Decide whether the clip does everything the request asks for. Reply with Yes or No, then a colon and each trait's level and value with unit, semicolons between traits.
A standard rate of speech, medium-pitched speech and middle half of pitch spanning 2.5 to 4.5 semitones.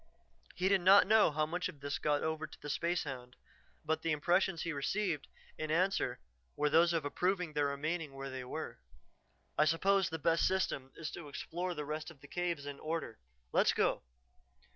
Yes: average, 185 wpm; medium, 160 Hz; average, 3.5 semitones